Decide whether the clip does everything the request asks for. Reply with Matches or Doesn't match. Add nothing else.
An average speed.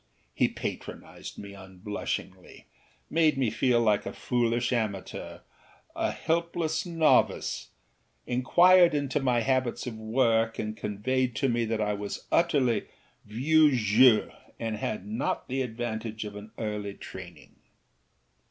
Doesn't match